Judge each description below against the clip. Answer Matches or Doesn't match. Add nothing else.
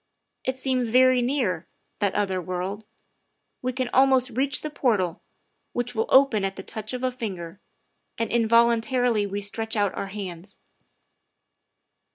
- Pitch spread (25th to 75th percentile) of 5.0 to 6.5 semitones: Doesn't match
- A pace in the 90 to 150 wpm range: Matches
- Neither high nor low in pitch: Doesn't match